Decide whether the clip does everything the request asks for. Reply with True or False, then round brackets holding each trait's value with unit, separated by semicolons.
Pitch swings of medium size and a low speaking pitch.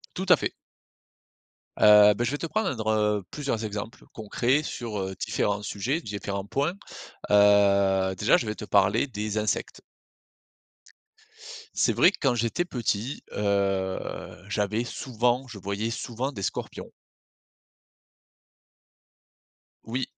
True (3.5 semitones; 105 Hz)